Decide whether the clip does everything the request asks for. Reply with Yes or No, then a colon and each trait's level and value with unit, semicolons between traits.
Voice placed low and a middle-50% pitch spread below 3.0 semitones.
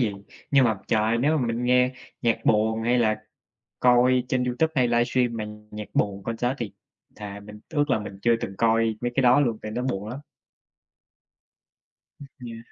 Yes: low, 115 Hz; narrow, 2.6 semitones